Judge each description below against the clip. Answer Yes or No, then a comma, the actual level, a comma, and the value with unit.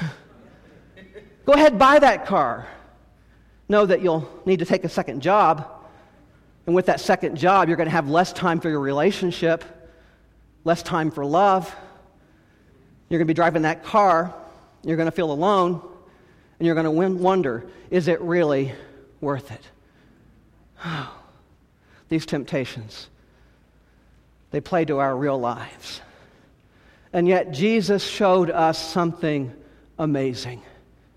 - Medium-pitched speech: Yes, medium, 165 Hz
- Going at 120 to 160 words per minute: Yes, slow, 135 wpm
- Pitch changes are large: No, average, 4.2 semitones